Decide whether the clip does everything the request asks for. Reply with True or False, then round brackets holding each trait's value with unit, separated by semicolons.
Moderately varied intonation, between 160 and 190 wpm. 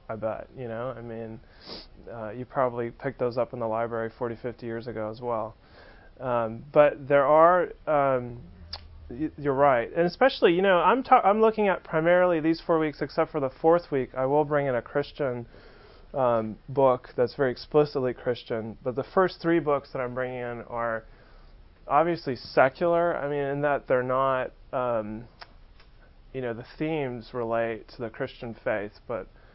True (4.5 semitones; 175 wpm)